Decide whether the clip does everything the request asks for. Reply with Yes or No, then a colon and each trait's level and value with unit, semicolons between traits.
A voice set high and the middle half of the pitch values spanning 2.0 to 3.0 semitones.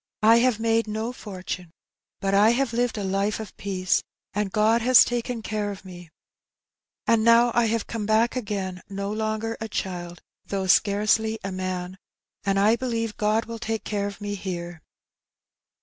Yes: high, 210 Hz; narrow, 2.6 semitones